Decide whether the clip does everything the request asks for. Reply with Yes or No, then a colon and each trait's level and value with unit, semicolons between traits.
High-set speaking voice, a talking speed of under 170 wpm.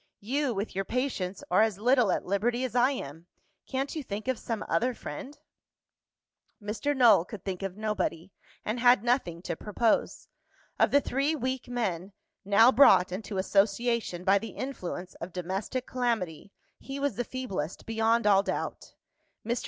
Yes: high, 220 Hz; average, 160 wpm